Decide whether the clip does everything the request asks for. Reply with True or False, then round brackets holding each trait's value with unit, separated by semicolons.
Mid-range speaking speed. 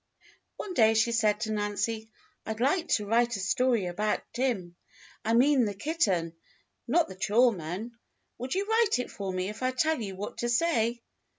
True (185 wpm)